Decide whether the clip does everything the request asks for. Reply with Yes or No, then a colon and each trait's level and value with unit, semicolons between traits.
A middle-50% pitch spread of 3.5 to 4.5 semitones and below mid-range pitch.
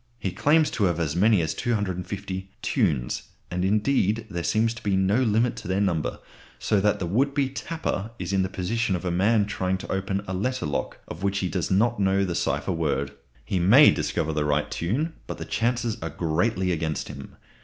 Yes: average, 4.2 semitones; very low, 95 Hz